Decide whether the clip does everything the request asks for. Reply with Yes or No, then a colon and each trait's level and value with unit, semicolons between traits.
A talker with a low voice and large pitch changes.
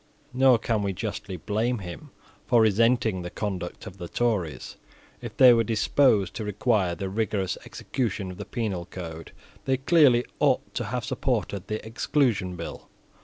No: low, 110 Hz; average, 4.4 semitones